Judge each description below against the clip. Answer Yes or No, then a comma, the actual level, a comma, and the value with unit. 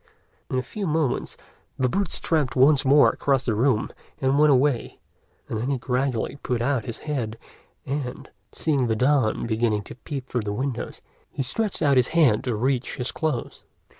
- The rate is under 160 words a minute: No, average, 180 wpm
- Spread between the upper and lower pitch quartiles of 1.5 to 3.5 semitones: Yes, average, 3.2 semitones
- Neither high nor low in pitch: No, low, 130 Hz